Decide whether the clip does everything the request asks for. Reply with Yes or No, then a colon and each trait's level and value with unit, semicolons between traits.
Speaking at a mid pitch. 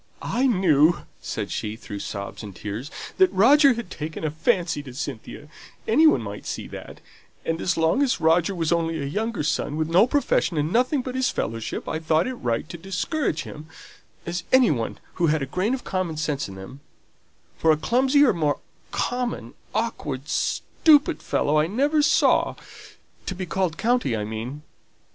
Yes: medium, 165 Hz